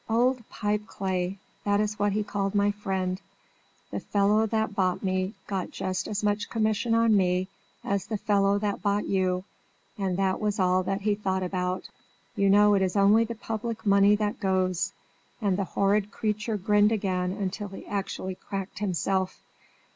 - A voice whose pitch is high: Yes, high, 200 Hz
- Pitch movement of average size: No, narrow, 1.9 semitones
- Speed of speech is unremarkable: Yes, average, 170 wpm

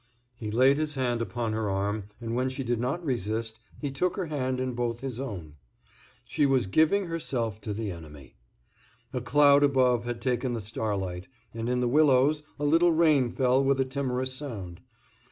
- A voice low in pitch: Yes, low, 125 Hz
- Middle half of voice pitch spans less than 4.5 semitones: Yes, average, 3.8 semitones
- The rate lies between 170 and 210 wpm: Yes, average, 185 wpm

